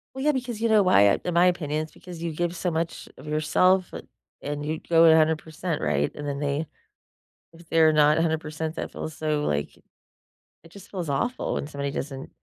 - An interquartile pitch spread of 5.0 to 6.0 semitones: No, average, 2.9 semitones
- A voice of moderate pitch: Yes, medium, 160 Hz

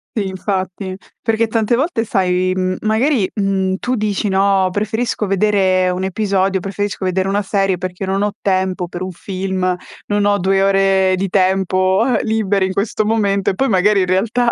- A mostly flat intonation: Yes, narrow, 1.9 semitones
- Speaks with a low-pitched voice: No, high, 195 Hz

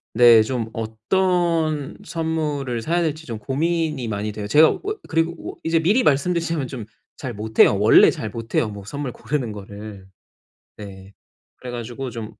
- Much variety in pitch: Yes, wide, 6.7 semitones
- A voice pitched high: No, low, 125 Hz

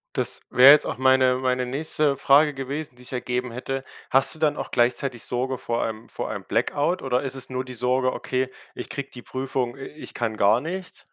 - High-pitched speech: No, low, 130 Hz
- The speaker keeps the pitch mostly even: Yes, narrow, 1.8 semitones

